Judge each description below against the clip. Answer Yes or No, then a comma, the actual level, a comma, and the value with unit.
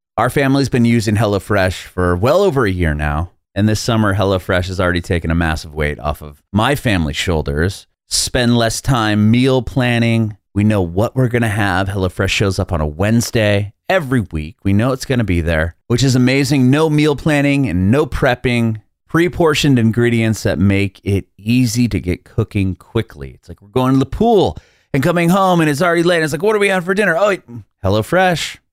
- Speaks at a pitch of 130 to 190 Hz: No, low, 110 Hz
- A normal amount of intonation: No, wide, 5.9 semitones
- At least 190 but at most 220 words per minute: Yes, average, 200 wpm